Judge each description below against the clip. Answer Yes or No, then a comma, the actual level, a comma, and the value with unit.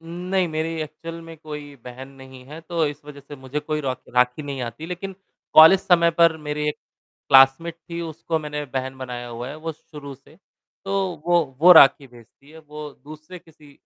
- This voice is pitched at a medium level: Yes, medium, 150 Hz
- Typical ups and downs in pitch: Yes, average, 3.4 semitones